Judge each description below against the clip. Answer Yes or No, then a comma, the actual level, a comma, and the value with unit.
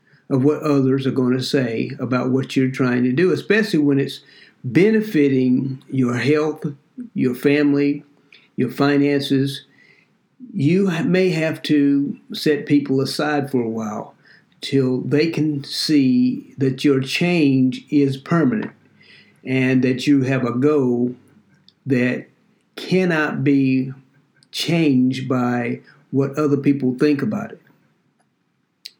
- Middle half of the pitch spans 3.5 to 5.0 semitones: No, narrow, 2.6 semitones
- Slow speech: Yes, slow, 120 wpm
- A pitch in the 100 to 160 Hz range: Yes, medium, 140 Hz